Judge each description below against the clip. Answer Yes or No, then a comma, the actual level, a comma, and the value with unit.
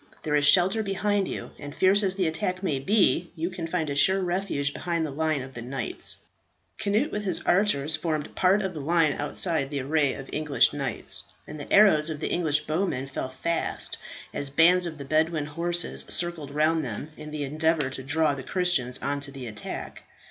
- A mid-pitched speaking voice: Yes, medium, 160 Hz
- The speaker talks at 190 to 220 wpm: Yes, average, 200 wpm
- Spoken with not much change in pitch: No, average, 4.0 semitones